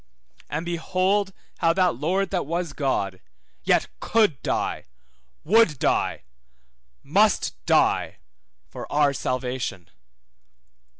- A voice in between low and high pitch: Yes, medium, 165 Hz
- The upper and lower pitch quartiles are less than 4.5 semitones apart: No, wide, 5.6 semitones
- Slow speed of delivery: Yes, slow, 100 wpm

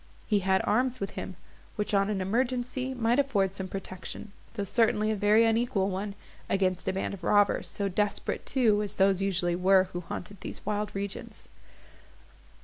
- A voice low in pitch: No, high, 200 Hz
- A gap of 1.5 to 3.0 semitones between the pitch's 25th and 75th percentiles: Yes, narrow, 2.5 semitones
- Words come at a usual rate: Yes, average, 170 wpm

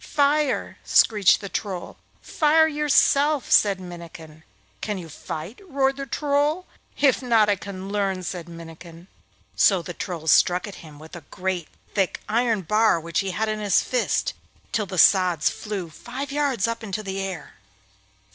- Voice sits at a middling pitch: No, high, 200 Hz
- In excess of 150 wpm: Yes, average, 160 wpm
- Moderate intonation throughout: No, wide, 6.2 semitones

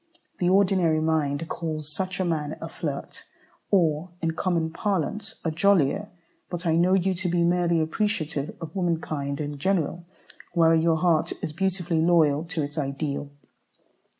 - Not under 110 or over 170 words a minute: Yes, average, 150 wpm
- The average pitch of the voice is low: No, medium, 165 Hz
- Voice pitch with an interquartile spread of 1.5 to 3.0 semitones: Yes, average, 2.7 semitones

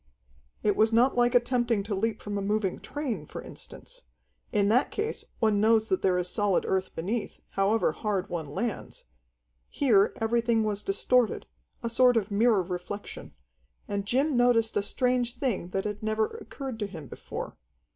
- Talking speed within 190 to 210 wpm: No, average, 165 wpm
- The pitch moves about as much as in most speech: Yes, average, 3.3 semitones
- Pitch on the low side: No, high, 215 Hz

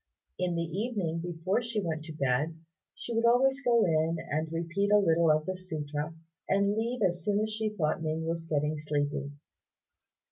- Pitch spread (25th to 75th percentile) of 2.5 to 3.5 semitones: No, average, 4.9 semitones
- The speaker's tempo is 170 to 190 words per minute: Yes, average, 180 wpm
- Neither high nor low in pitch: Yes, medium, 170 Hz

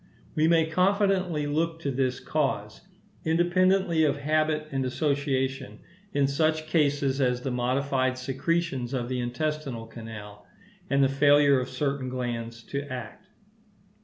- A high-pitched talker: No, medium, 140 Hz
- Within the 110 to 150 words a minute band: Yes, slow, 135 wpm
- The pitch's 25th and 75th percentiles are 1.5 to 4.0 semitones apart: Yes, average, 3.6 semitones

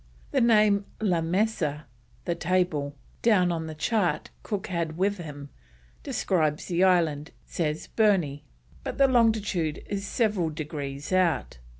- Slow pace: Yes, slow, 130 wpm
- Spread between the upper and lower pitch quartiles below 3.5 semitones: No, average, 4.8 semitones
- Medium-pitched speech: Yes, medium, 175 Hz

